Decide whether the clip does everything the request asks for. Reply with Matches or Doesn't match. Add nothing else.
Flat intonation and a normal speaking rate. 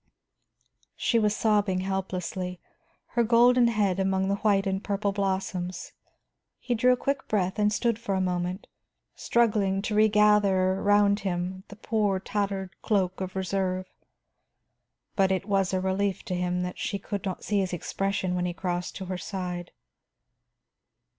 Matches